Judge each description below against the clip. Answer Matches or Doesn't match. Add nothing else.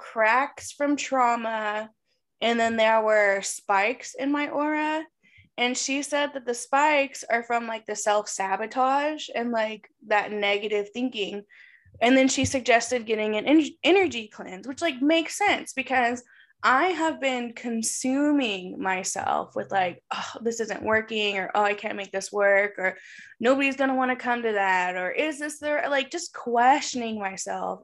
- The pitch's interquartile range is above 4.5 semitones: Matches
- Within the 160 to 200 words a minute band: Matches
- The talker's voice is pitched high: Matches